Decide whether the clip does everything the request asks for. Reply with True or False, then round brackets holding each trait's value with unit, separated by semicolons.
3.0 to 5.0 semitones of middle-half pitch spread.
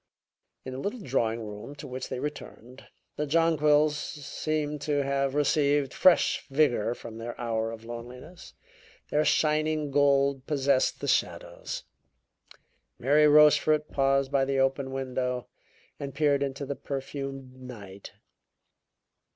False (2.6 semitones)